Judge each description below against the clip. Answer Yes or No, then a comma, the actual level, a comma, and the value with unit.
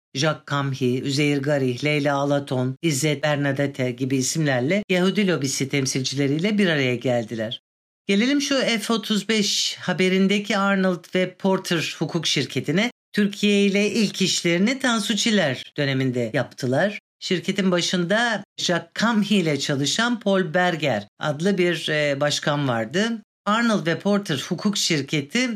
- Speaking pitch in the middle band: Yes, medium, 175 Hz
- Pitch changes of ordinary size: No, wide, 6.0 semitones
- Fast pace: No, average, 115 wpm